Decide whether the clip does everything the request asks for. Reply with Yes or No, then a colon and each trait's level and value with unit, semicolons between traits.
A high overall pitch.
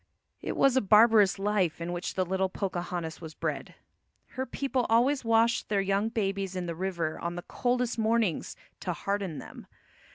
Yes: high, 195 Hz